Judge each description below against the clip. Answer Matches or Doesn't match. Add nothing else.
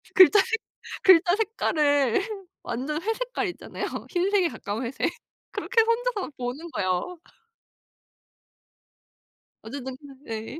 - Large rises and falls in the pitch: Matches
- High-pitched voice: Matches